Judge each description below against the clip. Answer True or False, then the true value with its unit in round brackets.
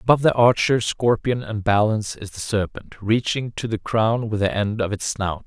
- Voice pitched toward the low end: True (110 Hz)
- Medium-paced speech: False (210 wpm)